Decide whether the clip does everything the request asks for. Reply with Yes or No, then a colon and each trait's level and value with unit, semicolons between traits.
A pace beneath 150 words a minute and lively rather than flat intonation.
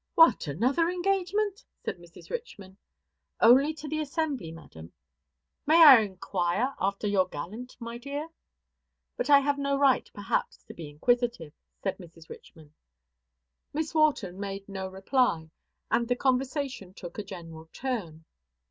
Yes: average, 140 wpm; wide, 7.8 semitones